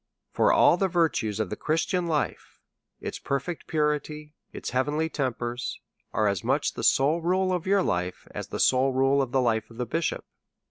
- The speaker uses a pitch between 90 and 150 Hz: Yes, medium, 140 Hz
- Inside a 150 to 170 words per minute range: No, average, 185 wpm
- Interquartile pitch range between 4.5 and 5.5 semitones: Yes, average, 5.1 semitones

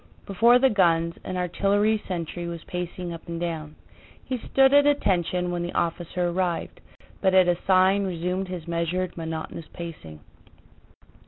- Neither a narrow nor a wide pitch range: No, narrow, 2.2 semitones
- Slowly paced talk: No, average, 150 wpm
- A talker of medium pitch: Yes, medium, 180 Hz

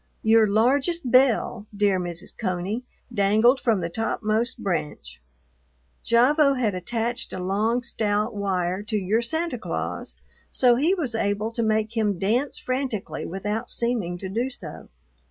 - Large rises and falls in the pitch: No, average, 3.6 semitones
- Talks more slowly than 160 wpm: Yes, average, 140 wpm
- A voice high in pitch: Yes, high, 220 Hz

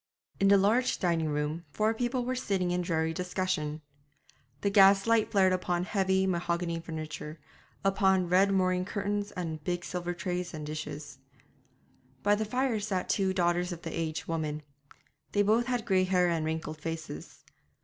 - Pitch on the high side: No, medium, 180 Hz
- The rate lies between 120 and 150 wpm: No, average, 165 wpm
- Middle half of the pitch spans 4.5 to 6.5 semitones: No, average, 3.5 semitones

